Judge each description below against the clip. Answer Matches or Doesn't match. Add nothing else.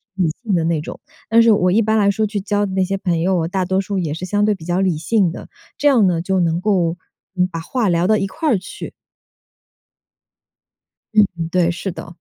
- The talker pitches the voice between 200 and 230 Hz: Doesn't match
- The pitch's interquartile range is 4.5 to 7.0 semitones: Doesn't match